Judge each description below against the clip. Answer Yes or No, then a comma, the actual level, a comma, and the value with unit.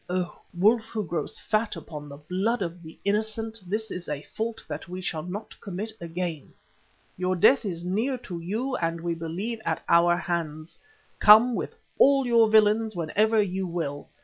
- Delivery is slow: No, average, 175 wpm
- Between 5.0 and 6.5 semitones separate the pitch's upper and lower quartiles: No, average, 4.6 semitones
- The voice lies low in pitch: No, medium, 185 Hz